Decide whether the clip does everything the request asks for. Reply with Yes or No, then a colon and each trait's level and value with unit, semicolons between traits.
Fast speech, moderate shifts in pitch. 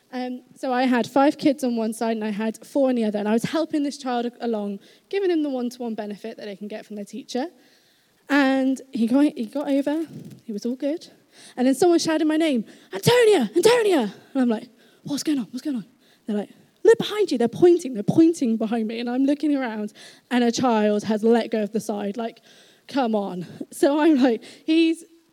Yes: fast, 225 wpm; average, 4.6 semitones